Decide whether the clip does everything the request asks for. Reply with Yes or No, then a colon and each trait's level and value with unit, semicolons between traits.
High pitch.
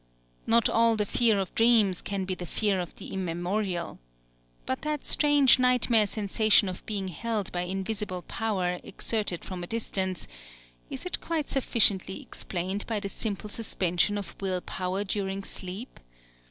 Yes: high, 200 Hz